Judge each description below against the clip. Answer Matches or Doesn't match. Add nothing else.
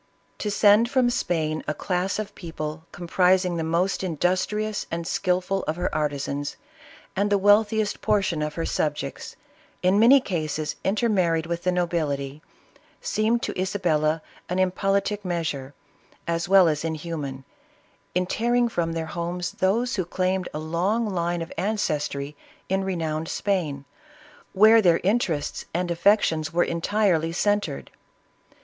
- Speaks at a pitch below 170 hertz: Doesn't match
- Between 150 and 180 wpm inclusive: Doesn't match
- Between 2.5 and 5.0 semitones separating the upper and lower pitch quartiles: Matches